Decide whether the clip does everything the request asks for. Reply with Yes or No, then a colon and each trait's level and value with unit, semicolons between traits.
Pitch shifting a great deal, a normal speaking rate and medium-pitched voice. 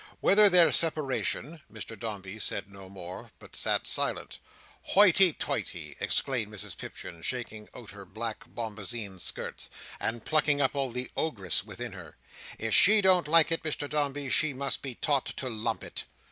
No: wide, 6.6 semitones; average, 160 wpm; low, 125 Hz